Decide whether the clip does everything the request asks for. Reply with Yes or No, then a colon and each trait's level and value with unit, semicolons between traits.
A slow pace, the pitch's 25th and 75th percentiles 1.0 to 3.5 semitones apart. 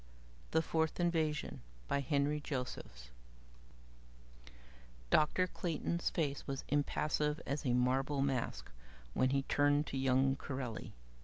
Yes: slow, 120 wpm; narrow, 2.4 semitones